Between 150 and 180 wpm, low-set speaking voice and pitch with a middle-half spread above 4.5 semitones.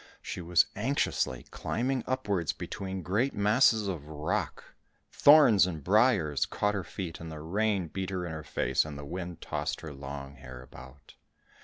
Yes: average, 155 wpm; very low, 90 Hz; wide, 5.6 semitones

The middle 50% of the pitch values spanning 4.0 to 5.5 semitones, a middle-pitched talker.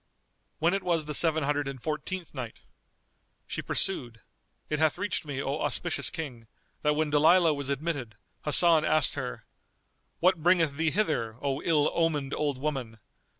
No: average, 3.0 semitones; medium, 150 Hz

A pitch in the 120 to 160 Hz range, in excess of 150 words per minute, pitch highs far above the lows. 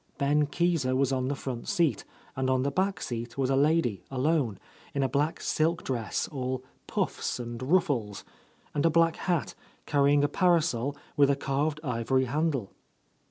No: medium, 140 Hz; average, 165 wpm; average, 3.2 semitones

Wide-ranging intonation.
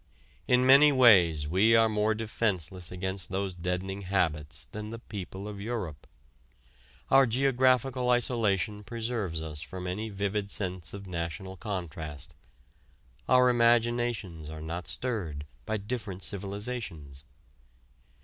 No: average, 4.8 semitones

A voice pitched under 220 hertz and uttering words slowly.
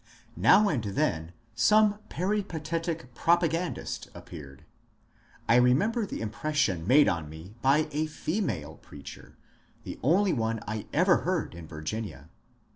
Yes: medium, 140 Hz; slow, 125 wpm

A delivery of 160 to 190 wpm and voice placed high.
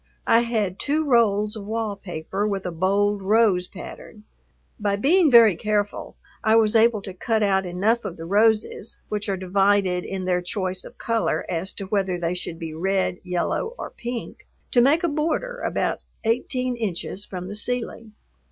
Yes: average, 175 wpm; high, 205 Hz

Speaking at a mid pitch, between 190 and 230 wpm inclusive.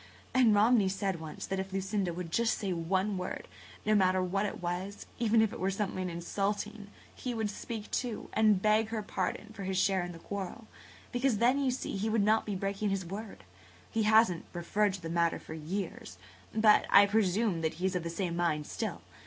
No: high, 200 Hz; fast, 205 wpm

